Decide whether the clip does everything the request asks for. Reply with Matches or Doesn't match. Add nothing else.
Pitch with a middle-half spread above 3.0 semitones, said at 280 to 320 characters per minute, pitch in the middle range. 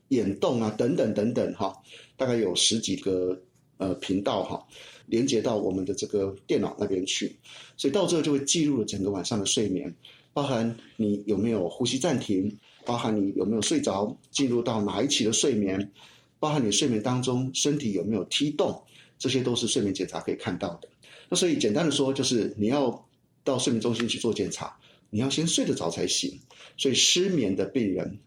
Doesn't match